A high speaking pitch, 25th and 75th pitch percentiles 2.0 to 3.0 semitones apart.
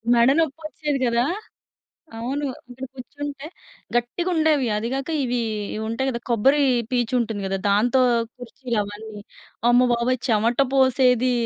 Yes: high, 245 Hz; narrow, 2.6 semitones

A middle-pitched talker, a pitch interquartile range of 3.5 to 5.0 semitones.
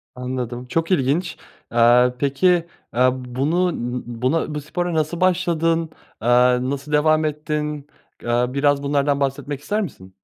Yes: medium, 145 Hz; average, 4.4 semitones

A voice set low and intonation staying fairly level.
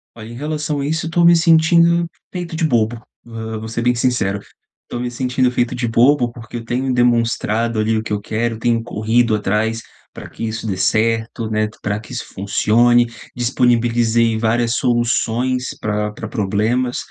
Yes: low, 120 Hz; narrow, 2.1 semitones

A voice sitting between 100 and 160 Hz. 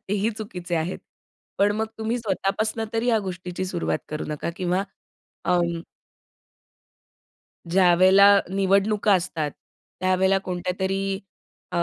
No: high, 190 Hz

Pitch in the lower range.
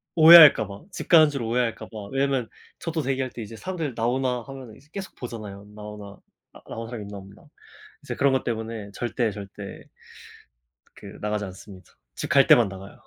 Yes: low, 115 Hz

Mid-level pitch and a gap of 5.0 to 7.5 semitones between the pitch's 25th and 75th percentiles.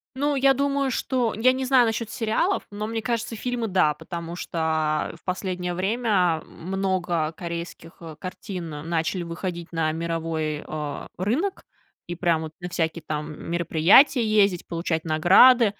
Yes: medium, 180 Hz; wide, 5.4 semitones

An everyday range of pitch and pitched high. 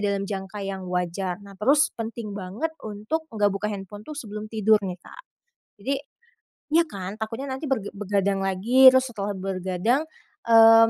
Yes: average, 3.2 semitones; high, 210 Hz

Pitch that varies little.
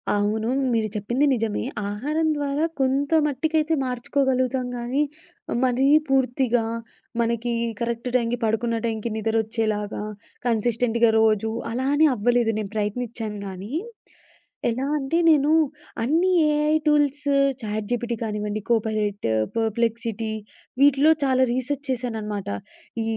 No: average, 3.4 semitones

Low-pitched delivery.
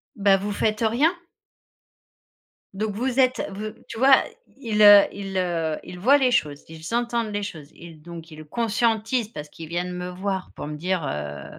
No: high, 200 Hz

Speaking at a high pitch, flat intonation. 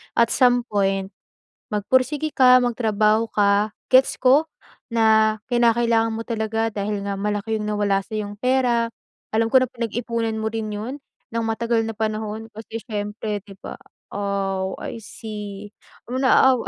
Yes: high, 220 Hz; narrow, 2.1 semitones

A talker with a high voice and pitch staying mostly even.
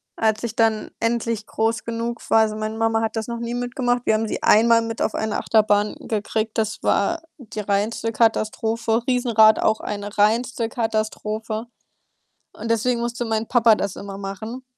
Yes: high, 225 Hz; narrow, 1.4 semitones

